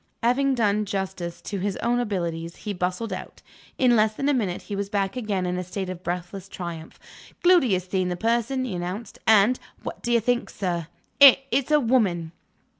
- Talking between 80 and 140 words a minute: No, average, 190 wpm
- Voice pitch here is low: No, high, 200 Hz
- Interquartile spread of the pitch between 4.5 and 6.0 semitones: Yes, average, 4.8 semitones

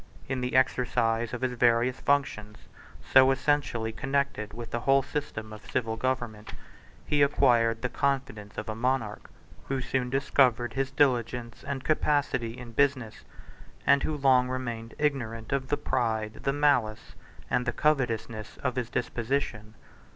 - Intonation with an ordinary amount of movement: Yes, average, 3.1 semitones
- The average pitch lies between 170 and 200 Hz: No, low, 125 Hz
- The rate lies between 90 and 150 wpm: Yes, average, 145 wpm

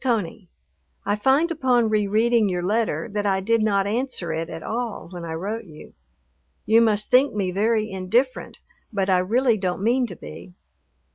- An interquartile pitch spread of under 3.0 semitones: No, average, 3.7 semitones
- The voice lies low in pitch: No, high, 215 Hz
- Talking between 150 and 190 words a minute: Yes, average, 180 wpm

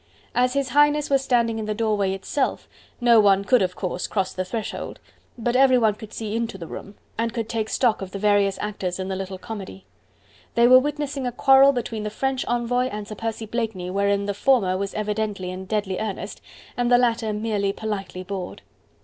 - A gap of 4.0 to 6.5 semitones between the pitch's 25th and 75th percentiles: No, average, 3.6 semitones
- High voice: Yes, high, 215 Hz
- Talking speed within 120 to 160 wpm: No, average, 200 wpm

